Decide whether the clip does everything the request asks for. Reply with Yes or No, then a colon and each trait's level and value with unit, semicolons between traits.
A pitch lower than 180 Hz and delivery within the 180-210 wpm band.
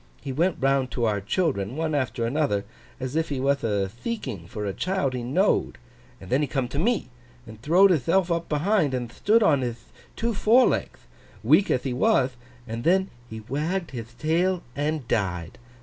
Yes: medium, 140 Hz; average, 185 wpm